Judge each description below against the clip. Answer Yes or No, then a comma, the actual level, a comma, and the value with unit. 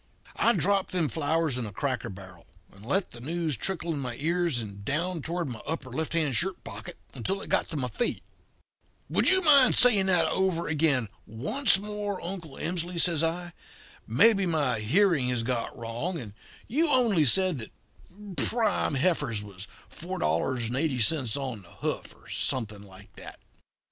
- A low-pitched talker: No, medium, 155 Hz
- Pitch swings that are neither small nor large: No, wide, 7.6 semitones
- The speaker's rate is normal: Yes, average, 165 wpm